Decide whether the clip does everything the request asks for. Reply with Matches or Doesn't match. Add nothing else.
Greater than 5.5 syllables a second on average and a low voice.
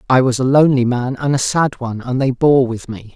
Matches